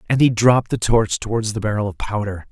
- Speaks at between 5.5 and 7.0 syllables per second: Yes, 6.0 syllables/s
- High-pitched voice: No, low, 110 Hz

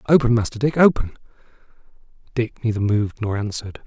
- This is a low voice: Yes, low, 115 Hz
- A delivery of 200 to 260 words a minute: No, average, 140 wpm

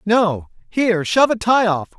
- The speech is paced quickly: No, average, 150 wpm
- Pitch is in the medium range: No, high, 205 Hz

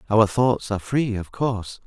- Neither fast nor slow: Yes, average, 195 wpm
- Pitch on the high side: No, low, 110 Hz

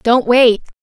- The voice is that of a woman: Yes, female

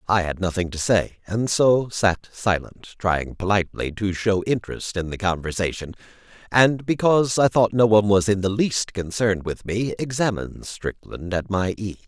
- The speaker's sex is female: No, male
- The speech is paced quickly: No, average, 175 wpm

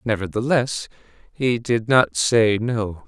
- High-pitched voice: No, low, 115 Hz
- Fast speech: No, slow, 115 wpm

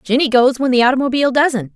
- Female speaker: Yes, female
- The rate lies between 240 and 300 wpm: No, fast, 205 wpm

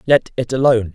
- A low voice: Yes, low, 125 Hz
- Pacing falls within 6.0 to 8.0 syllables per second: Yes, 6.4 syllables/s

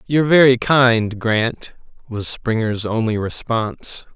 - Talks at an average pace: No, slow, 115 wpm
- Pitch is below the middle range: Yes, low, 115 Hz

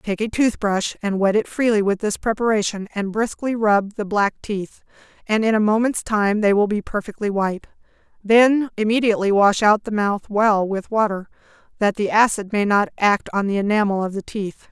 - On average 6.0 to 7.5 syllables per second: No, 5.1 syllables/s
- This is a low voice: No, high, 210 Hz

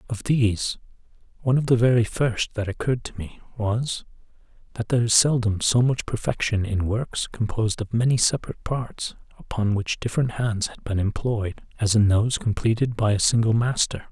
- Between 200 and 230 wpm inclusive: No, average, 175 wpm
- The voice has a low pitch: Yes, low, 110 Hz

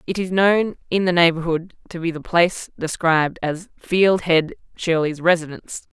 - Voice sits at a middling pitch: Yes, medium, 170 Hz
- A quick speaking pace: No, average, 160 wpm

